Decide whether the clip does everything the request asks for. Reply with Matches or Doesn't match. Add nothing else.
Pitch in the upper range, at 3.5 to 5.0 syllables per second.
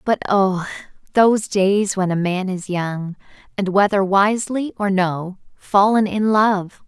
Matches